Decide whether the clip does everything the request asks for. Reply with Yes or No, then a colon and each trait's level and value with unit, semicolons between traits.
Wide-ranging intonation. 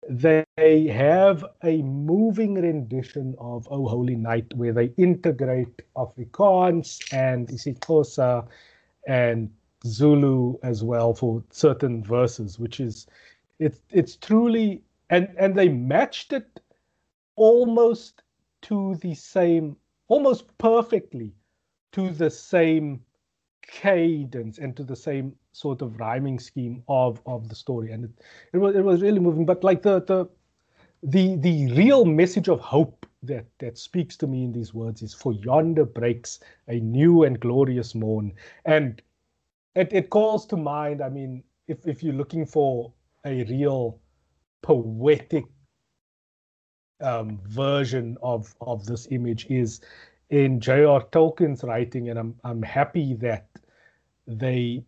Yes: wide, 5.7 semitones